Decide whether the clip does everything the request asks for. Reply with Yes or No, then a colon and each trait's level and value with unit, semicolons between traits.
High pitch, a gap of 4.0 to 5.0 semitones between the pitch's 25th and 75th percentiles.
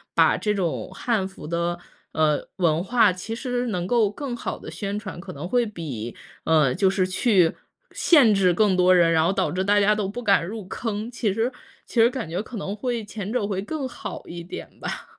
Yes: high, 200 Hz; average, 4.5 semitones